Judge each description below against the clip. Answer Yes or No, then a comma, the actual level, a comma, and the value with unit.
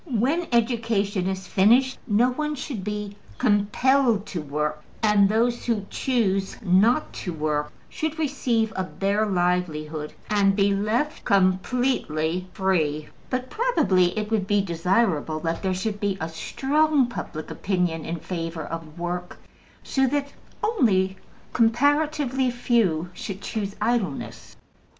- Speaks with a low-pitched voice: No, high, 205 Hz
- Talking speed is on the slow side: Yes, slow, 130 wpm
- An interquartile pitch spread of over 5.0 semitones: Yes, wide, 5.4 semitones